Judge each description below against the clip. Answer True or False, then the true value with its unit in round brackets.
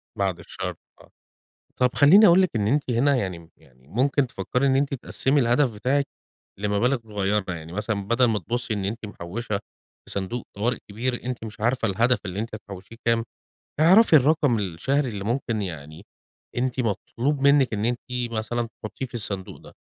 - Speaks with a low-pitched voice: True (115 Hz)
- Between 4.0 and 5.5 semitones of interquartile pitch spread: True (4.3 semitones)